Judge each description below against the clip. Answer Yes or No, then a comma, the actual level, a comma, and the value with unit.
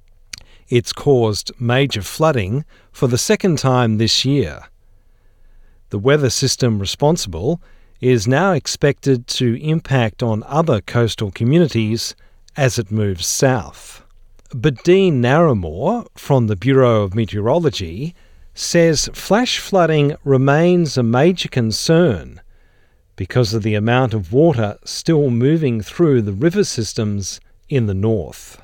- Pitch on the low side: Yes, low, 120 Hz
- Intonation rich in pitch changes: Yes, wide, 5.7 semitones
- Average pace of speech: No, slow, 120 wpm